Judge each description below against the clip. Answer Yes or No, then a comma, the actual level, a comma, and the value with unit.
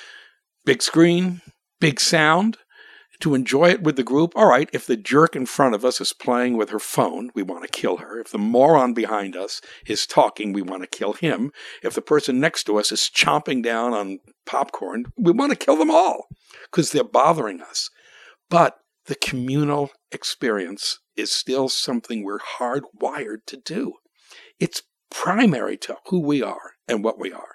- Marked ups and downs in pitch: Yes, wide, 7.2 semitones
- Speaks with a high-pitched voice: No, medium, 140 Hz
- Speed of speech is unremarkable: Yes, average, 180 wpm